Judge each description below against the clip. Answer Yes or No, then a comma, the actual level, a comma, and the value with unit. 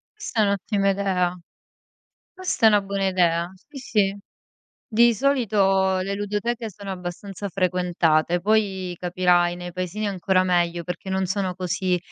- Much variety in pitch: No, narrow, 2.4 semitones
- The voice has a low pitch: No, high, 190 Hz